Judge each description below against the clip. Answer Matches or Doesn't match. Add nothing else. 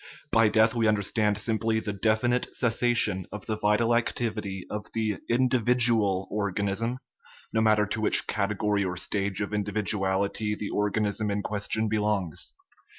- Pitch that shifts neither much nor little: Doesn't match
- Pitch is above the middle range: Doesn't match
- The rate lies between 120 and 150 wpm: Matches